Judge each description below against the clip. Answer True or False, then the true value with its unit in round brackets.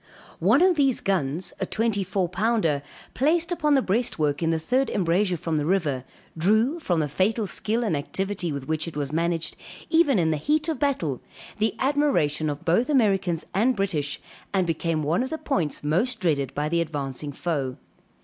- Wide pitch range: True (7.1 semitones)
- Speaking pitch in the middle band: True (180 Hz)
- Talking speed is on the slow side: False (185 wpm)